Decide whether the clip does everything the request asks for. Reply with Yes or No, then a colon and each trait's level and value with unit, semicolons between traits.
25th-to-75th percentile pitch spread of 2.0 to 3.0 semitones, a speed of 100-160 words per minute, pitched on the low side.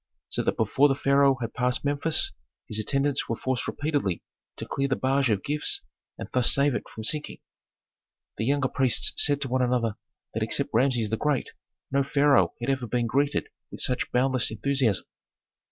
No: average, 2.7 semitones; average, 180 wpm; low, 130 Hz